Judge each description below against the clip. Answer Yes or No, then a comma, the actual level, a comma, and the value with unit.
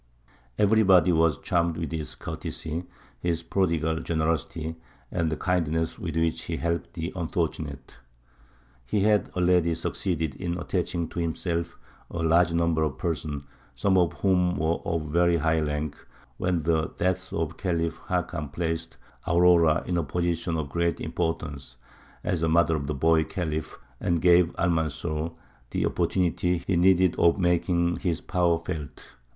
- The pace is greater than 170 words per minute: No, average, 145 wpm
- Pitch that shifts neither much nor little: No, narrow, 1.7 semitones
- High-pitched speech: No, very low, 85 Hz